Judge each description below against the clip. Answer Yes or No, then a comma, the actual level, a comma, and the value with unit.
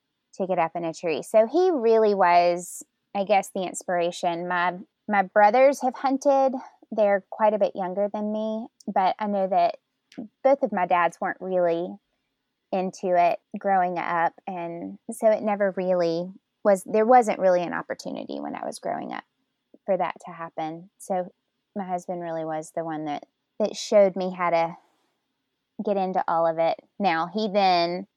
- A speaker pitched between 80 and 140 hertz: No, high, 190 Hz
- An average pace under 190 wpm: Yes, average, 175 wpm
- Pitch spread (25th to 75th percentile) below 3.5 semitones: No, average, 3.8 semitones